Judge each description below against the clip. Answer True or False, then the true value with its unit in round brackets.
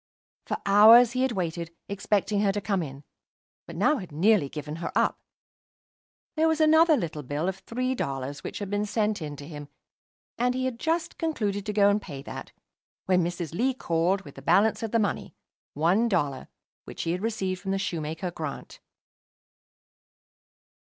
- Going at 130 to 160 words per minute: False (180 wpm)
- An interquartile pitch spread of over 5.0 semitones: True (5.4 semitones)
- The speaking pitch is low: False (195 Hz)